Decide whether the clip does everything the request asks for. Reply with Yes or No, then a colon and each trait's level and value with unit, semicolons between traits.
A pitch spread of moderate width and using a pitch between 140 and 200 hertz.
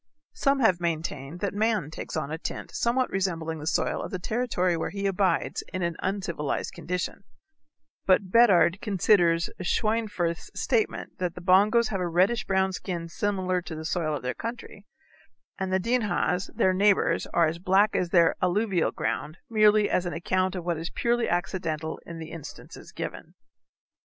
Yes: average, 3.4 semitones; medium, 185 Hz